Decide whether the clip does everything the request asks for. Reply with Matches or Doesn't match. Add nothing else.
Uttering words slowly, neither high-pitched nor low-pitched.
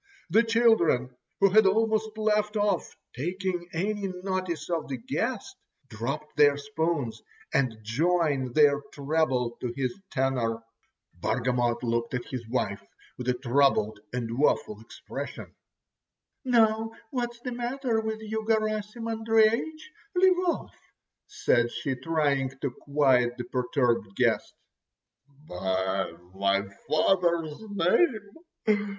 Matches